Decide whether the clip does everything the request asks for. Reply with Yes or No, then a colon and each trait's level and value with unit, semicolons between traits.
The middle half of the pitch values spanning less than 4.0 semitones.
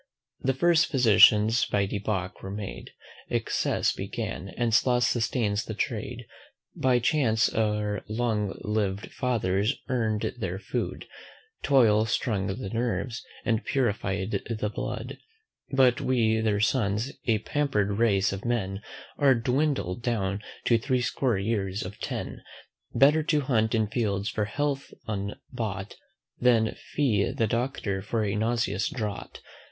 Yes: average, 3.3 semitones